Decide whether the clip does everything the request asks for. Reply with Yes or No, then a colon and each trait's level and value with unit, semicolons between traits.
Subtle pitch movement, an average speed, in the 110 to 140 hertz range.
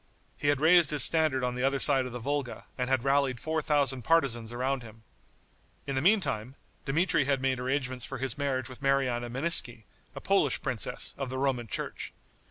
Yes: narrow, 2.3 semitones; average, 190 wpm; low, 135 Hz